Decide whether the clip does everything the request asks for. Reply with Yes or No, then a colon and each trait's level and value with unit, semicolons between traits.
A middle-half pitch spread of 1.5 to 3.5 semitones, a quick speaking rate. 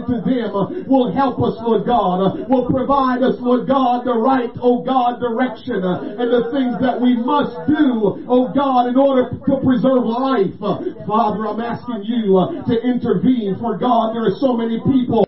No: narrow, 2.4 semitones; average, 175 wpm